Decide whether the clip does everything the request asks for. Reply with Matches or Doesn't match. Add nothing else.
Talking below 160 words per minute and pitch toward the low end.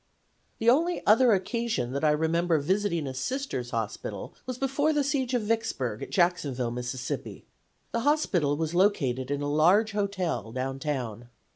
Doesn't match